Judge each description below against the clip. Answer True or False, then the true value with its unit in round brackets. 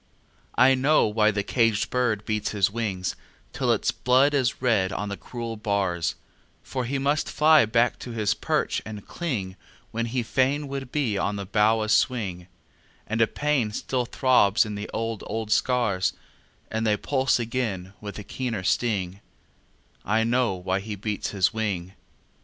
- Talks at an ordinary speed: True (170 wpm)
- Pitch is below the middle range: True (110 Hz)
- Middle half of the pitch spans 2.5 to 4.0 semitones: True (3.7 semitones)